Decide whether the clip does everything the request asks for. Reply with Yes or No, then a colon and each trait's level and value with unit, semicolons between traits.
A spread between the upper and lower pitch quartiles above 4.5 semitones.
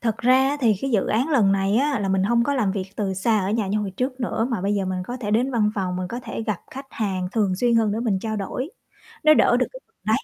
No: average, 4.0 semitones